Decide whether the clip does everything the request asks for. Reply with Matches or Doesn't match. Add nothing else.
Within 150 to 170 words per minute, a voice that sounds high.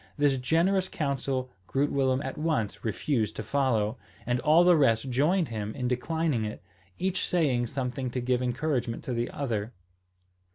Doesn't match